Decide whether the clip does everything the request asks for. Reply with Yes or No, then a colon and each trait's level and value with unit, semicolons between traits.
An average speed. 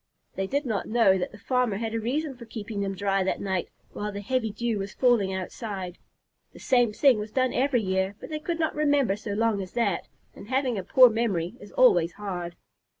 No: fast, 215 wpm